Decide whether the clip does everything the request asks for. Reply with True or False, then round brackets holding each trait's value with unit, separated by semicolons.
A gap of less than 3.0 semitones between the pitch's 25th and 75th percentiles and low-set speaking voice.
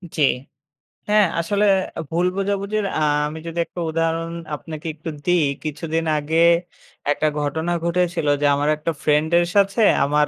False (2.6 semitones; 165 Hz)